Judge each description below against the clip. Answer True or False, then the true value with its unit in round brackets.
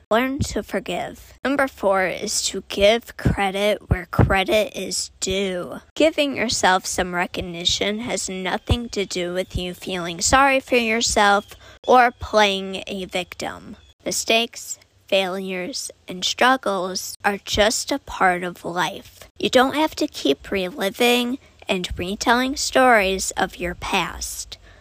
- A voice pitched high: True (195 Hz)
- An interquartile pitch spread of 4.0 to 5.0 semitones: True (4.3 semitones)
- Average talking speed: False (130 wpm)